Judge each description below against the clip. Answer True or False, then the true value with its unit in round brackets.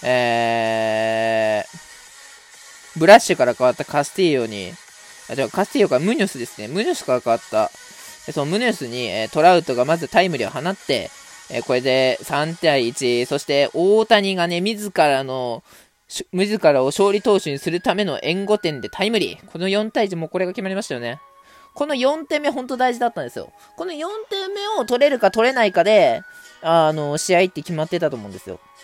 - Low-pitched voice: False (175 Hz)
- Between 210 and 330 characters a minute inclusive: False (370 characters per minute)